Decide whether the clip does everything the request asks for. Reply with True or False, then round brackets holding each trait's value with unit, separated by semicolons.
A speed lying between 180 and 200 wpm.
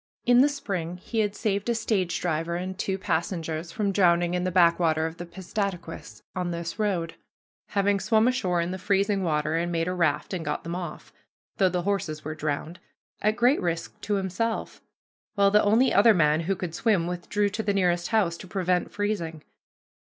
True (190 wpm)